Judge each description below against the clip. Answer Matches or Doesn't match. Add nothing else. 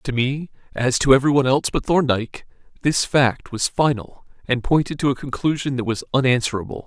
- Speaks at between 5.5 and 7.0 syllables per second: Matches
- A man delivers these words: Matches